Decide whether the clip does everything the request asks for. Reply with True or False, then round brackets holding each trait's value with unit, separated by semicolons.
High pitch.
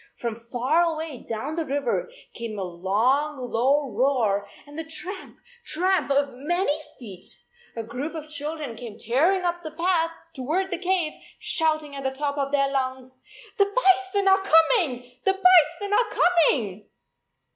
True (290 Hz)